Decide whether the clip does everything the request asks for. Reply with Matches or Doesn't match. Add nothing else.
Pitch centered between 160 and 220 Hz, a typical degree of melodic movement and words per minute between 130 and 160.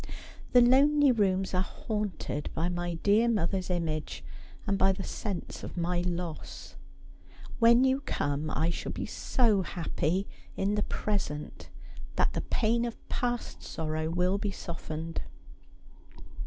Matches